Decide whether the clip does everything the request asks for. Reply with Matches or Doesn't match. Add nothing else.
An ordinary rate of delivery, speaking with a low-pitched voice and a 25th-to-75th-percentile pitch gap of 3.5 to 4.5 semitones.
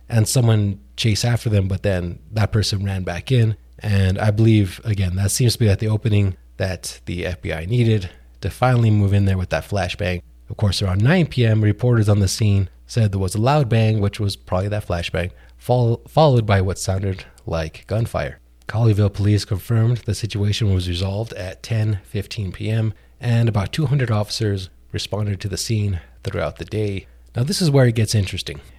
Doesn't match